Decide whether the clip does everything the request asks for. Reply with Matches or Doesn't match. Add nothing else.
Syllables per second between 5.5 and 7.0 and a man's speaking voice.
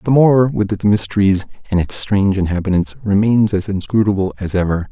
Matches